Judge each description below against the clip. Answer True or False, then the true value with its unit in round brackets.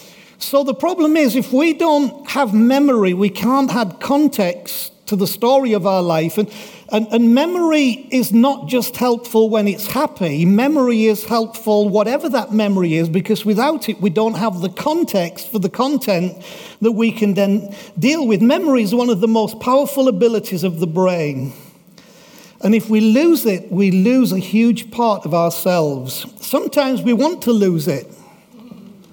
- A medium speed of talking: True (170 wpm)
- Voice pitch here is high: True (220 Hz)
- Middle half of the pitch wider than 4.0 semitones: True (4.6 semitones)